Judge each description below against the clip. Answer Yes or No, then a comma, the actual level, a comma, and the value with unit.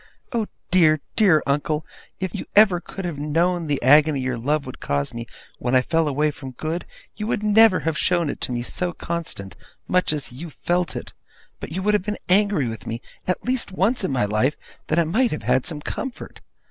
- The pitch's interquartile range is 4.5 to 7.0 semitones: Yes, average, 5.1 semitones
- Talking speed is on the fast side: Yes, fast, 210 wpm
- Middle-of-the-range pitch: Yes, medium, 160 Hz